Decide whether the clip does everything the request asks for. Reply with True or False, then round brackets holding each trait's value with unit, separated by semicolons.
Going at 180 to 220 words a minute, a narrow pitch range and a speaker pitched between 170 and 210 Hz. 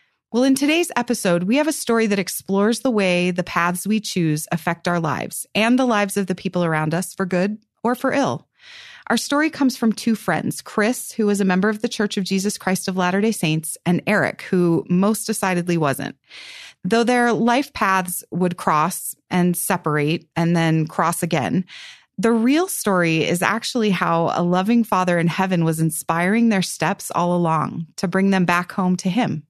False (195 wpm; 4.8 semitones; 190 Hz)